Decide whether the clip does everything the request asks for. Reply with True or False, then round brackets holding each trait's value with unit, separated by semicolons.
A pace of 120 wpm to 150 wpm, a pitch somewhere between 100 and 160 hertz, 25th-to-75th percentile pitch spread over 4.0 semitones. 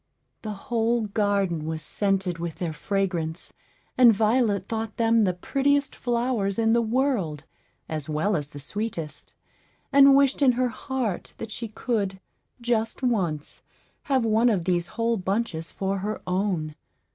False (145 wpm; 210 Hz; 4.7 semitones)